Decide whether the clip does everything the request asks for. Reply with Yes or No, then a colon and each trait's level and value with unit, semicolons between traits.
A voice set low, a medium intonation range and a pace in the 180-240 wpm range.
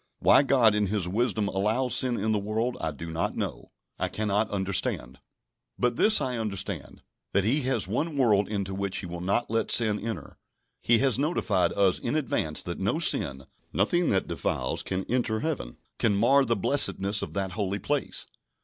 Yes: low, 105 Hz; average, 4.0 semitones; average, 185 wpm